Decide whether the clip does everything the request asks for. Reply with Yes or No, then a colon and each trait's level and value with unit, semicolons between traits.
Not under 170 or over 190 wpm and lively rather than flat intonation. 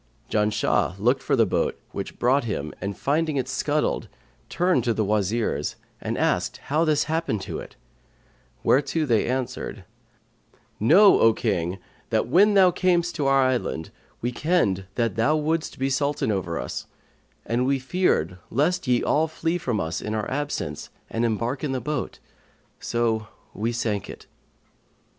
No: average, 160 wpm; wide, 6.0 semitones